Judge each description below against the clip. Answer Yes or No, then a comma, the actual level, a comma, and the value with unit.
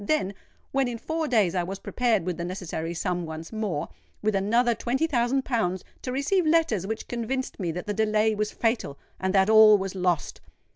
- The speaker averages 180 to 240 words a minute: Yes, average, 185 wpm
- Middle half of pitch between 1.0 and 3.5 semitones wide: No, average, 4.9 semitones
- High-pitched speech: Yes, high, 215 Hz